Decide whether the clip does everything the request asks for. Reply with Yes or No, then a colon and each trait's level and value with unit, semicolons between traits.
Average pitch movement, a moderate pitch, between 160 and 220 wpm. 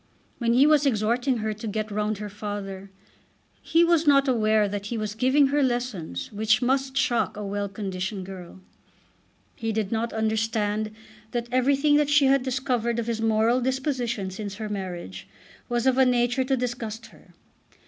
No: average, 3.8 semitones; high, 225 Hz; average, 170 wpm